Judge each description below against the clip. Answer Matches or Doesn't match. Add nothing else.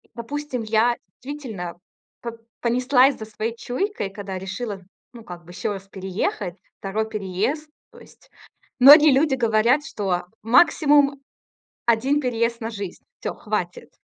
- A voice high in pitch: Matches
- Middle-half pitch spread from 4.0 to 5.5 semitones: Matches